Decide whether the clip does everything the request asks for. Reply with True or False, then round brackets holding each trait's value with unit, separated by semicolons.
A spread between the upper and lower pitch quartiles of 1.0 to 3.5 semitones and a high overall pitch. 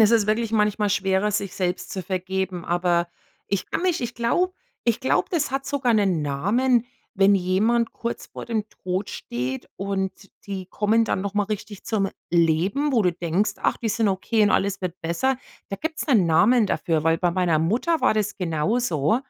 False (4.2 semitones; 200 Hz)